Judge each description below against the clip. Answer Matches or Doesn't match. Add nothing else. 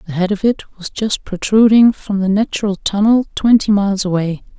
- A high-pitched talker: Matches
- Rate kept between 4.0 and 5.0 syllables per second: Doesn't match